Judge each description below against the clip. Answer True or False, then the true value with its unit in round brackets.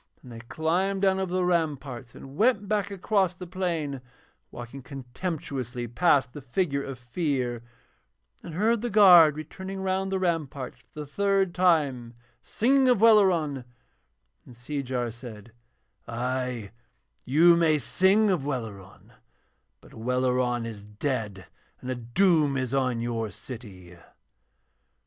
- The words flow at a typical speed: False (130 wpm)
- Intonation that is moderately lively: False (7.2 semitones)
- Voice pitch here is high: False (140 Hz)